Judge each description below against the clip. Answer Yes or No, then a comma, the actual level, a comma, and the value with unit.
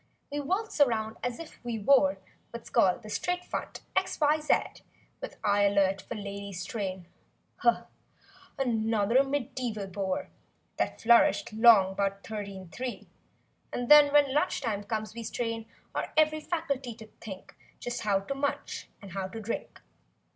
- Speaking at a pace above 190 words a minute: No, average, 150 wpm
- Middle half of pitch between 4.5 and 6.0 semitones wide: Yes, wide, 5.6 semitones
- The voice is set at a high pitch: Yes, high, 230 Hz